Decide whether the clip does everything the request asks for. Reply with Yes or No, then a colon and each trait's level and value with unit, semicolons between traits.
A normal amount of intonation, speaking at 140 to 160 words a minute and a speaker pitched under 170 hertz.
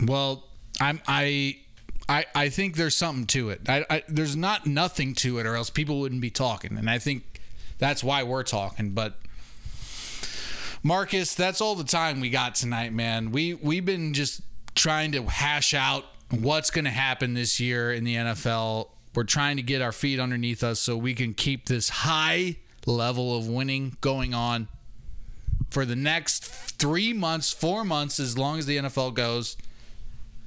No: average, 4.0 semitones; average, 175 wpm; low, 135 Hz